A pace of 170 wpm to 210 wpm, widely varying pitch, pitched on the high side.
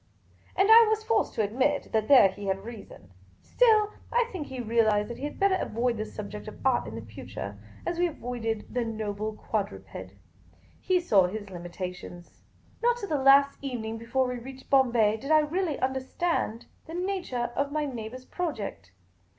Yes: average, 175 wpm; wide, 6.3 semitones; high, 245 Hz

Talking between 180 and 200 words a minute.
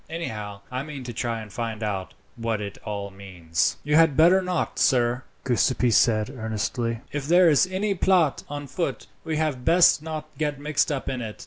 Yes: average, 190 wpm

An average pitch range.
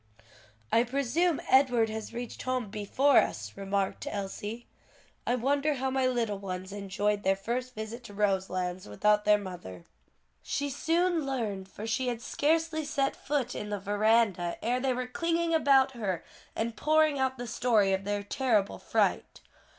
Yes: average, 4.8 semitones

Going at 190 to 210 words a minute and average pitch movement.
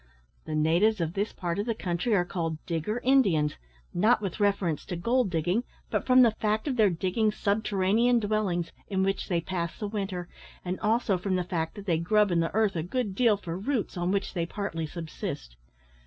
Yes: average, 200 wpm; average, 3.9 semitones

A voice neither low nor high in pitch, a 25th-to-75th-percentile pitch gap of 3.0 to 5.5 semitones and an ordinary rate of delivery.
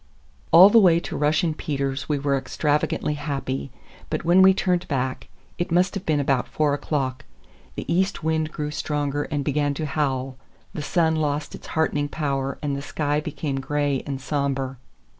No: medium, 145 Hz; narrow, 2.4 semitones; average, 165 wpm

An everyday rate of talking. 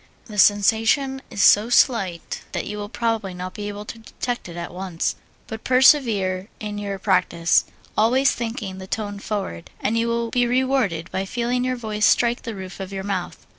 Yes: average, 185 wpm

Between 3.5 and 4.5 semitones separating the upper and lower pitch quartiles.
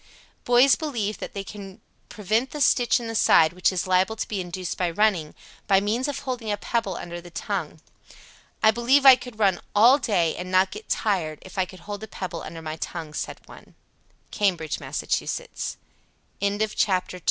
Yes: average, 4.1 semitones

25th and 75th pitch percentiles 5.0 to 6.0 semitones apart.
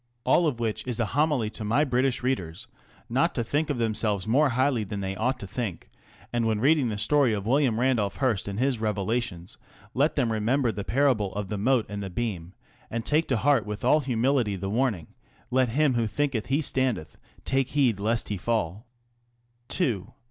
No: average, 4.2 semitones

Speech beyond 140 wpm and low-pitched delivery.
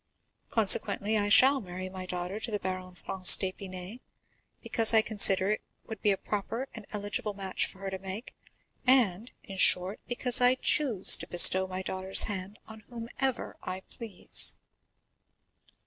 No: average, 155 wpm; high, 200 Hz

